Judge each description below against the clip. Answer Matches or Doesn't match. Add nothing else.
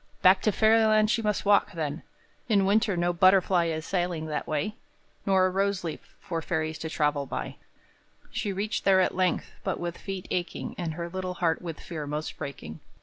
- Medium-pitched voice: Matches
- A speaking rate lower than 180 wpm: Doesn't match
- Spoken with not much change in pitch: Doesn't match